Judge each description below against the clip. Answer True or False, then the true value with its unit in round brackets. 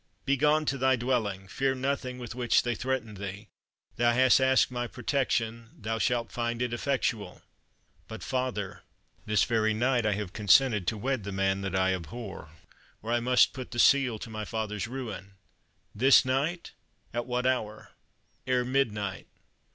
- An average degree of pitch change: True (3.5 semitones)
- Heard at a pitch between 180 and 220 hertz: False (120 Hz)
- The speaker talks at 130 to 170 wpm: True (160 wpm)